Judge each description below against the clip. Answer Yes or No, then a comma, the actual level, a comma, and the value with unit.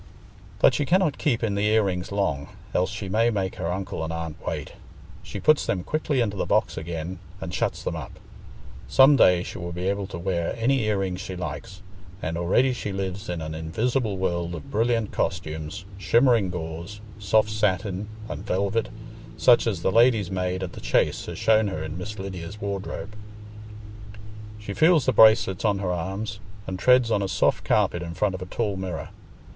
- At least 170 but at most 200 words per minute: Yes, average, 190 wpm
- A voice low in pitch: Yes, very low, 95 Hz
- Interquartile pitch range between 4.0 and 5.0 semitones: No, average, 3.5 semitones